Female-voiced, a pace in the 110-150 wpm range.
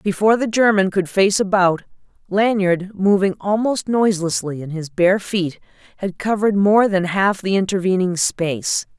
Yes: female; average, 145 wpm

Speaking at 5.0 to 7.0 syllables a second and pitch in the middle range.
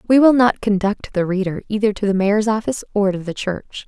No: 5.7 syllables/s; high, 205 Hz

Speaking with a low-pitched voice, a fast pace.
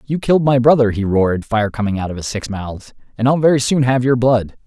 Yes: low, 120 Hz; fast, 255 wpm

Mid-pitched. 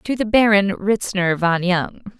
No: high, 200 Hz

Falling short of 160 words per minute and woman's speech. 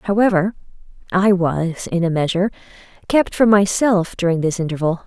Yes: average, 140 wpm; female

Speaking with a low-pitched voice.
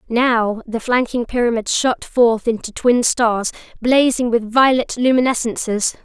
No: high, 235 Hz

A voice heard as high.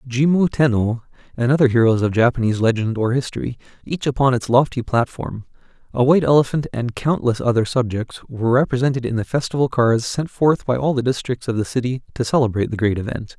No: low, 125 Hz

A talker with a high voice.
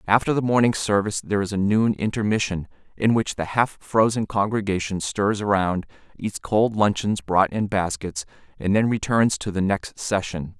No: low, 100 Hz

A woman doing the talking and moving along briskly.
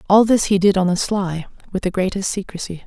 Yes: female; fast, 230 wpm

